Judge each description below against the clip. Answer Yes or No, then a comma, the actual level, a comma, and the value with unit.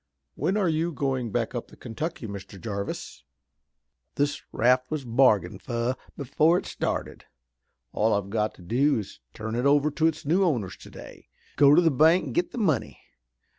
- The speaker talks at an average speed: Yes, average, 180 wpm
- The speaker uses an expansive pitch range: Yes, wide, 5.9 semitones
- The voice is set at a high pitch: No, low, 135 Hz